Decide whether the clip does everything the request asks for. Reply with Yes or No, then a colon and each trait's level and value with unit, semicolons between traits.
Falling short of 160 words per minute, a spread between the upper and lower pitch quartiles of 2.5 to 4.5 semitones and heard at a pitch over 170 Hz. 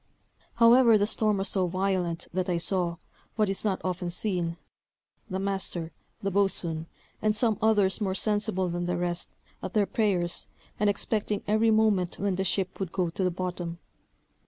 No: average, 170 wpm; average, 2.9 semitones; high, 190 Hz